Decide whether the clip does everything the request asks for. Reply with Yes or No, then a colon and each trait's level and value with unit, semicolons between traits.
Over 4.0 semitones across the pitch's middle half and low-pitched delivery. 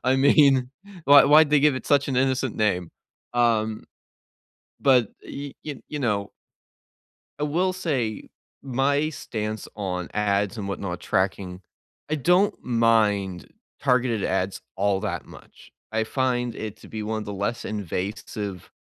Yes: average, 5.2 semitones; low, 115 Hz